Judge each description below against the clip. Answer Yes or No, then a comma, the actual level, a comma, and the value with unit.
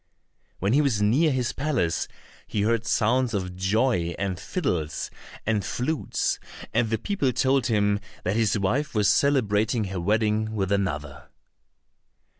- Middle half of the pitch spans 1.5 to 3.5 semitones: No, average, 4.5 semitones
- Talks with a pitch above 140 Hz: No, low, 110 Hz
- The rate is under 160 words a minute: Yes, average, 140 wpm